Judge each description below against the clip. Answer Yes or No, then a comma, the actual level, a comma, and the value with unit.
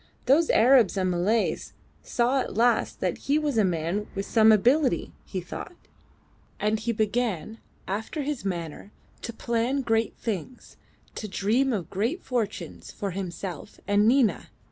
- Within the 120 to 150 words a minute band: Yes, average, 145 wpm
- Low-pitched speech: No, high, 220 Hz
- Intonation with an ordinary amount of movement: Yes, average, 4.1 semitones